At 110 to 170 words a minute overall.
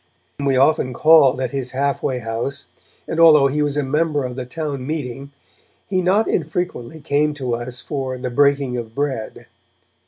No: average, 180 wpm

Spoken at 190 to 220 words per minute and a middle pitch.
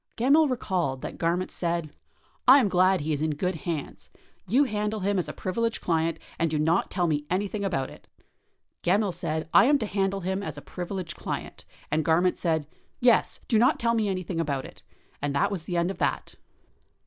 Yes: average, 200 wpm; medium, 180 Hz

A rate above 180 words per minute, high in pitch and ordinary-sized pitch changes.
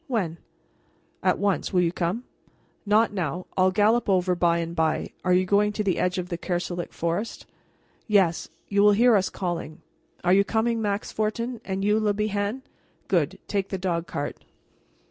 No: average, 175 wpm; high, 195 Hz; average, 3.0 semitones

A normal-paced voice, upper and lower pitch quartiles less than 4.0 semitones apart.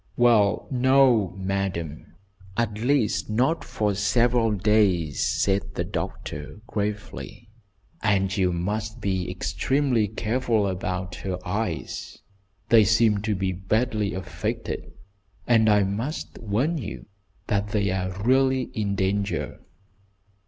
No: slow, 115 wpm; average, 3.4 semitones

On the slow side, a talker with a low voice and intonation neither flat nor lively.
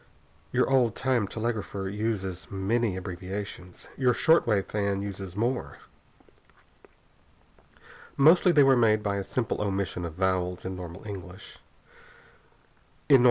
Yes: slow, 120 wpm; low, 100 Hz; average, 3.9 semitones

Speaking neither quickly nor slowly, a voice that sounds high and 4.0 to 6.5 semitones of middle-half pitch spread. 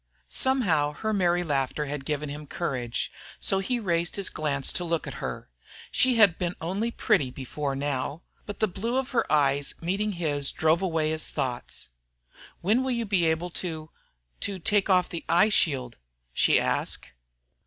No: average, 170 wpm; medium, 170 Hz; wide, 5.4 semitones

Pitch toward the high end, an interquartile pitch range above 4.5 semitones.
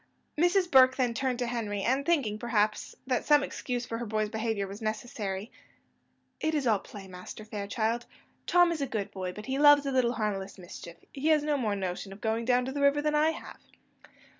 Yes: high, 235 Hz; average, 5.0 semitones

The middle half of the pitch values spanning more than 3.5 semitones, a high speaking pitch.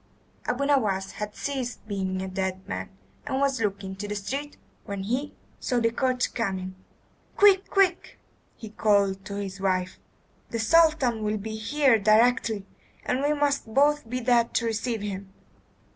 Yes: average, 5.0 semitones; high, 225 Hz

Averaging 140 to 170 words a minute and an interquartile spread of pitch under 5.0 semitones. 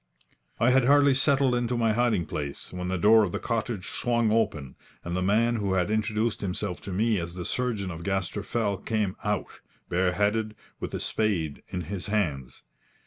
No: average, 185 wpm; average, 4.1 semitones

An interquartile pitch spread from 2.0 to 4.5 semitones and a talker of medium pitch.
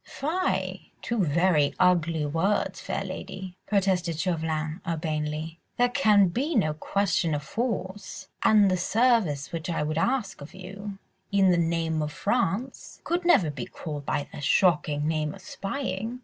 No: average, 4.9 semitones; medium, 180 Hz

